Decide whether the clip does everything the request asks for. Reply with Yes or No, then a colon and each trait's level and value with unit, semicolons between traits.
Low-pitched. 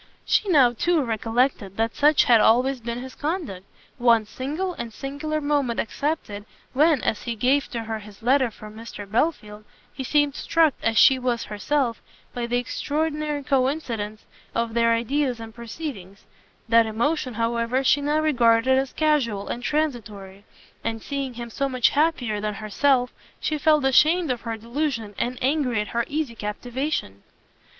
No: high, 245 Hz